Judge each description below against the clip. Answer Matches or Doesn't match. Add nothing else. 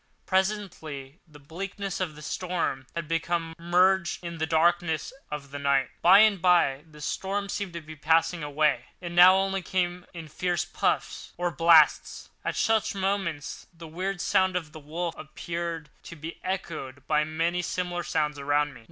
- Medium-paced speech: Matches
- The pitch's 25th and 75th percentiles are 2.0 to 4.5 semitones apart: Matches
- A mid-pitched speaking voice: Matches